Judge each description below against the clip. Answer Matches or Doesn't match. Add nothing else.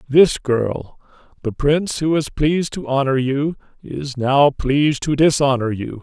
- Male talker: Matches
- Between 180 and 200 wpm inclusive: Doesn't match